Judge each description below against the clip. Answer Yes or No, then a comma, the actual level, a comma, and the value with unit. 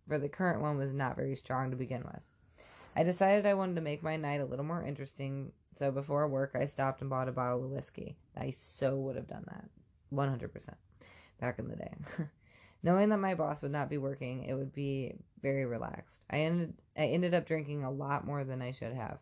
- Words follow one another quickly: Yes, fast, 220 wpm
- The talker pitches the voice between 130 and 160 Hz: Yes, medium, 140 Hz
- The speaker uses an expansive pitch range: No, average, 3.3 semitones